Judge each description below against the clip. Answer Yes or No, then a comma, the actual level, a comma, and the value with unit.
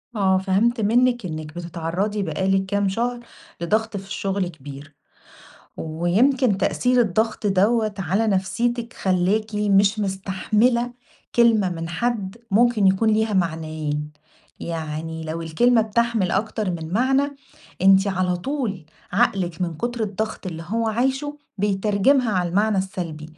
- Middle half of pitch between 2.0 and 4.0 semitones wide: No, average, 4.4 semitones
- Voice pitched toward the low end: No, high, 195 Hz